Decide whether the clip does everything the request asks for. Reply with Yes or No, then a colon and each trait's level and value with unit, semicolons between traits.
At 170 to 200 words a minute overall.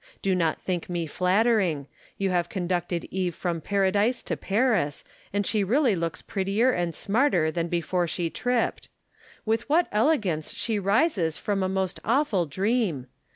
No: average, 155 wpm